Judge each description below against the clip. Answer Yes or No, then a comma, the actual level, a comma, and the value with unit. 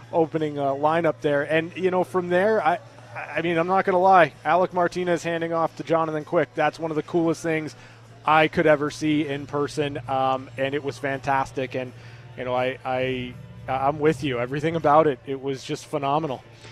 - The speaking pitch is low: No, medium, 150 Hz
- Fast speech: No, average, 195 wpm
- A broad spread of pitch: No, average, 3.5 semitones